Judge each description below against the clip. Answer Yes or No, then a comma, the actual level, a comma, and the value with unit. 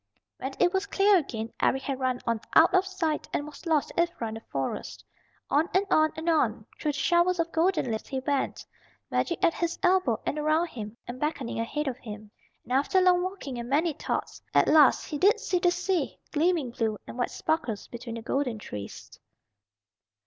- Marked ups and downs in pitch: Yes, wide, 6.1 semitones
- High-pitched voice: Yes, very high, 295 Hz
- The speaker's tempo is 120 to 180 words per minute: No, average, 200 wpm